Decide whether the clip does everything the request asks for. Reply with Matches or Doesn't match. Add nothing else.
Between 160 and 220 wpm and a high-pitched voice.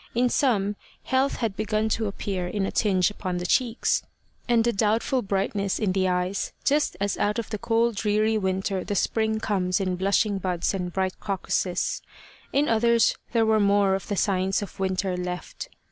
Matches